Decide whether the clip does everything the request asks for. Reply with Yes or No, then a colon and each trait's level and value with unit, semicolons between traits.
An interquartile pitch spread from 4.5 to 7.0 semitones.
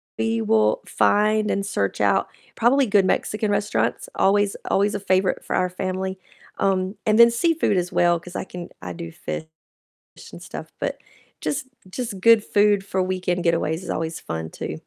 No: average, 3.2 semitones